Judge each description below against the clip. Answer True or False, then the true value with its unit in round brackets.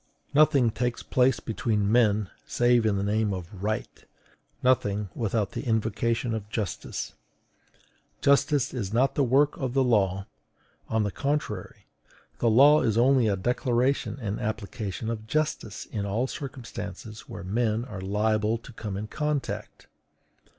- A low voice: True (115 Hz)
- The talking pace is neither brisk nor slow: True (145 wpm)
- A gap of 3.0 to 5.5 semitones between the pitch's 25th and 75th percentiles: True (3.5 semitones)